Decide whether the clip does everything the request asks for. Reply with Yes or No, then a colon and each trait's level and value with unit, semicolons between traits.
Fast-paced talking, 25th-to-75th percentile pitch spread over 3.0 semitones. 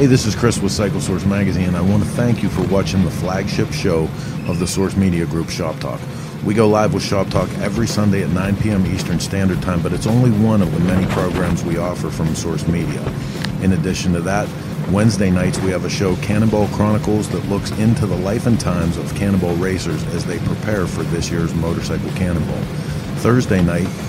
No: fast, 210 wpm; narrow, 2.6 semitones